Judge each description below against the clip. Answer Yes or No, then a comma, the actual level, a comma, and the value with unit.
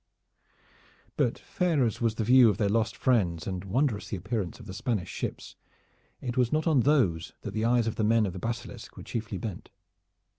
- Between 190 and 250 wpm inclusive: Yes, average, 200 wpm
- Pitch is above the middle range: No, low, 115 Hz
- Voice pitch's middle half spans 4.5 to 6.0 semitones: No, average, 3.6 semitones